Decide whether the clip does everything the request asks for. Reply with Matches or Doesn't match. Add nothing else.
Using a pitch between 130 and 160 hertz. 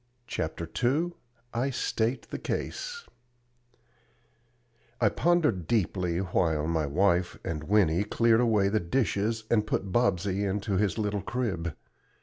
Doesn't match